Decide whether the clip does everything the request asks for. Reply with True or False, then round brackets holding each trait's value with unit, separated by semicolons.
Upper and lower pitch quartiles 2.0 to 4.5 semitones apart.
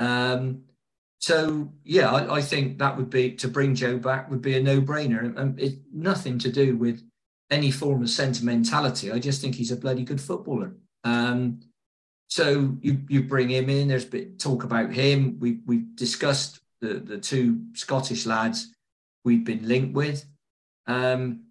True (2.5 semitones)